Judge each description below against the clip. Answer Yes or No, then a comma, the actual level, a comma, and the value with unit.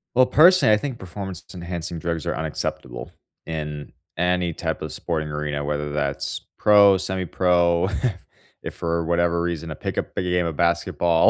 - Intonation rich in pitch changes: No, average, 2.9 semitones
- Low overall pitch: Yes, very low, 85 Hz